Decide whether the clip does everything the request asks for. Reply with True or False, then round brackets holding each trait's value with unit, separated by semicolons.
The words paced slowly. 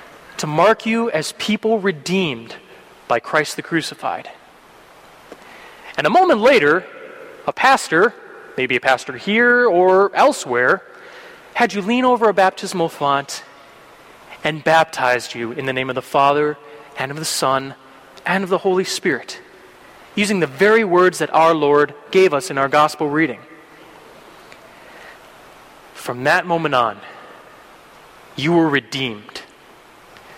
True (130 wpm)